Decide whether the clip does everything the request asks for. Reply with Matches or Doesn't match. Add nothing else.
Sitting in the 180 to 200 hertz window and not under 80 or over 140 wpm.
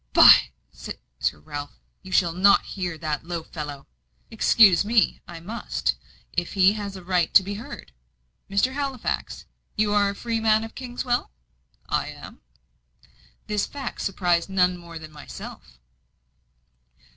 Matches